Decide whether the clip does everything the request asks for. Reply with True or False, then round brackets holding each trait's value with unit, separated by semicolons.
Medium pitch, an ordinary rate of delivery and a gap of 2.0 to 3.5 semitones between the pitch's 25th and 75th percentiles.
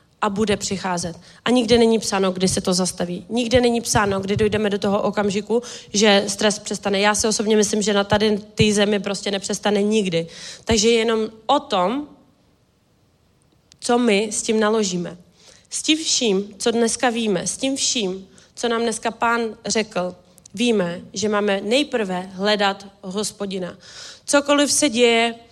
False (210 Hz; 155 wpm; 2.7 semitones)